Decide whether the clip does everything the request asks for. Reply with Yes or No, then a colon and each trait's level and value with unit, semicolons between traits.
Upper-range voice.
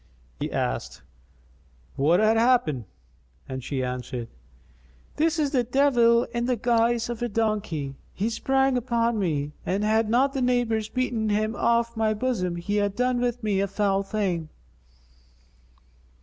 Yes: high, 220 Hz